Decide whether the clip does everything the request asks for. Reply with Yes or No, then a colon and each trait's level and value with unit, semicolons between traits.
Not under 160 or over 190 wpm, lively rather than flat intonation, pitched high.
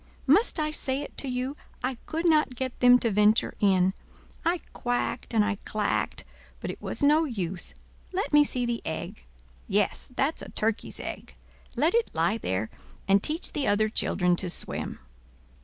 Yes: average, 175 wpm; wide, 6.4 semitones; high, 245 Hz